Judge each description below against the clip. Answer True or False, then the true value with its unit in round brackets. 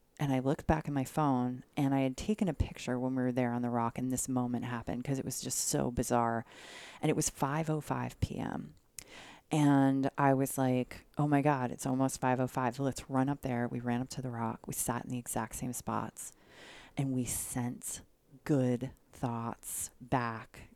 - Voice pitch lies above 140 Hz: False (130 Hz)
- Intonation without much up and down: True (2.2 semitones)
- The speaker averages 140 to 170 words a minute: False (200 wpm)